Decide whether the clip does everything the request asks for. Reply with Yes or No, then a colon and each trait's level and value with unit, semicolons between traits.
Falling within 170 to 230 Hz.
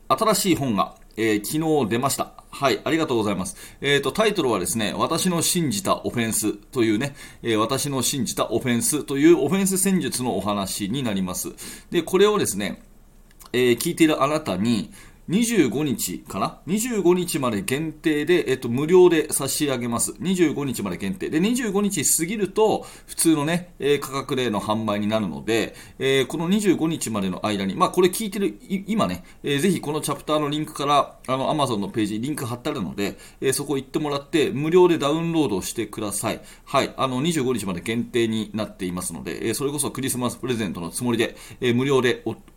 No: medium, 140 Hz